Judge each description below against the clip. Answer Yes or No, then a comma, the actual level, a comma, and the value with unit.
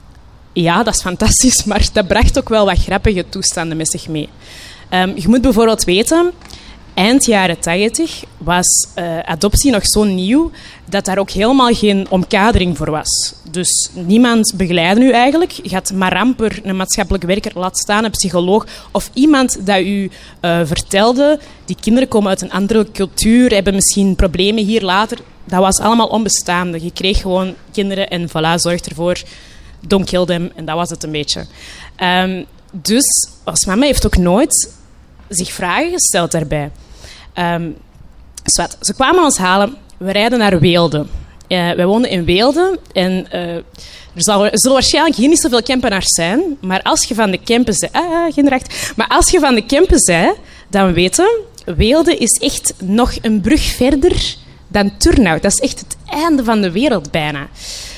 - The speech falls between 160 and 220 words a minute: Yes, average, 170 wpm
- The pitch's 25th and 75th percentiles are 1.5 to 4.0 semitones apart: No, wide, 5.4 semitones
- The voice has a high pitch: Yes, high, 195 Hz